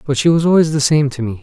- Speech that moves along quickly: Yes, fast, 335 wpm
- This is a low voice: No, medium, 145 Hz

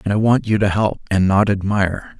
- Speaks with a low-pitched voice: Yes, low, 100 Hz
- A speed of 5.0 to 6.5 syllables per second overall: Yes, 5.6 syllables/s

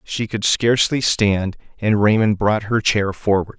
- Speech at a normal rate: Yes, average, 165 wpm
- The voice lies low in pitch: Yes, low, 105 Hz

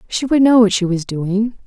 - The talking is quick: Yes, fast, 255 wpm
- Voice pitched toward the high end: Yes, high, 215 Hz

